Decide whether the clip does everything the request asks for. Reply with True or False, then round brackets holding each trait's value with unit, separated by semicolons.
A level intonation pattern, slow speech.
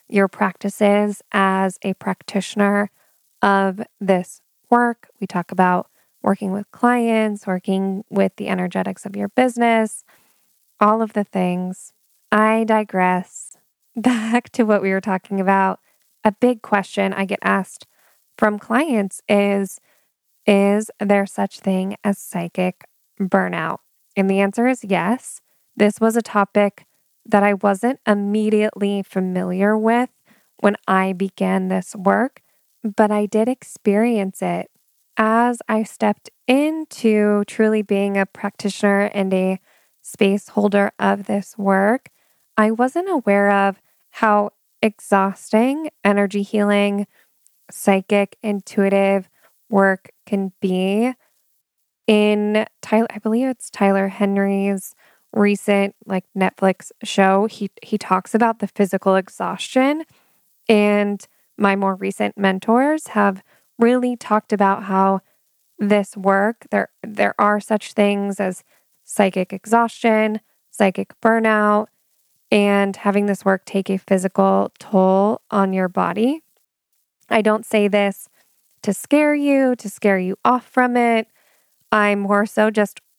True (2.1 semitones; 125 wpm)